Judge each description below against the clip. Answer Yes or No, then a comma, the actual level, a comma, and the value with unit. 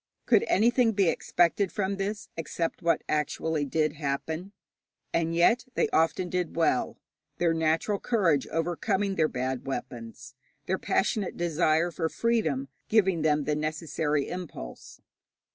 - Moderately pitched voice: Yes, medium, 165 Hz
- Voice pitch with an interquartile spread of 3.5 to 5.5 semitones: Yes, average, 4.0 semitones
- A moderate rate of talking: No, slow, 130 wpm